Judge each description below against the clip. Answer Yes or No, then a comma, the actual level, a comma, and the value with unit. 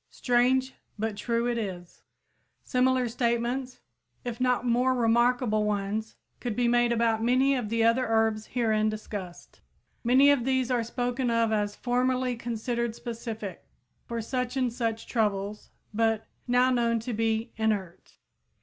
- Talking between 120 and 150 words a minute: Yes, average, 140 wpm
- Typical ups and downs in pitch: No, narrow, 2.1 semitones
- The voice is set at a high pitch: Yes, high, 235 Hz